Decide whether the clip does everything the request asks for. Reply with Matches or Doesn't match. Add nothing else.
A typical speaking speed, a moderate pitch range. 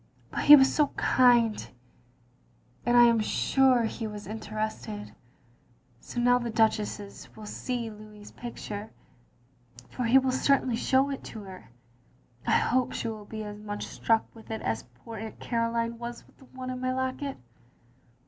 Matches